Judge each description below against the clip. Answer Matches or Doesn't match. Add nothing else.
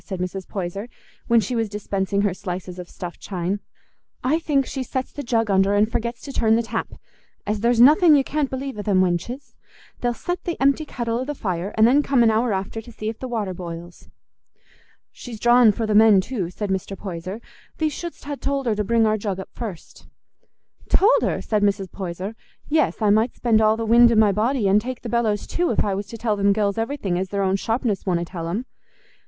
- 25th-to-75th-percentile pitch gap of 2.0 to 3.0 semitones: Doesn't match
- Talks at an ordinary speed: Doesn't match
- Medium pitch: Doesn't match